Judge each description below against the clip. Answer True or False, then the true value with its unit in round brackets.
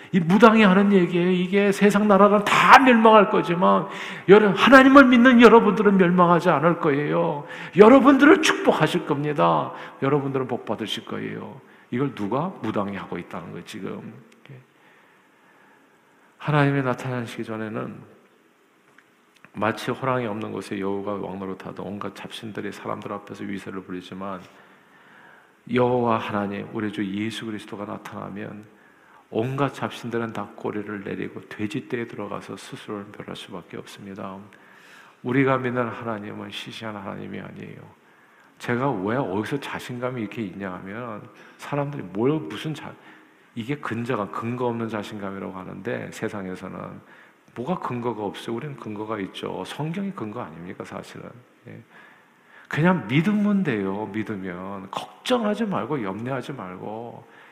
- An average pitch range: False (8.7 semitones)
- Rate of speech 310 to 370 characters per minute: True (315 characters per minute)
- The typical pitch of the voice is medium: False (120 Hz)